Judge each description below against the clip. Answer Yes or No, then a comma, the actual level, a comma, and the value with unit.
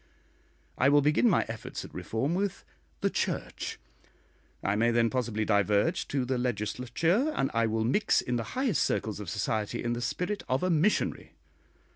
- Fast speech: No, average, 170 wpm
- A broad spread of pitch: Yes, wide, 6.9 semitones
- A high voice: No, low, 125 Hz